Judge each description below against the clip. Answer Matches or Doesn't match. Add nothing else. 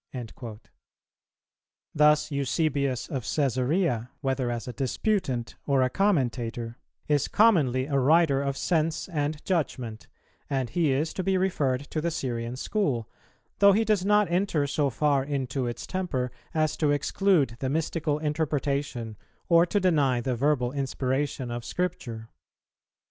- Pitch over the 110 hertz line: Matches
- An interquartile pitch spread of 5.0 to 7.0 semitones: Doesn't match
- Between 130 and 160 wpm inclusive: Matches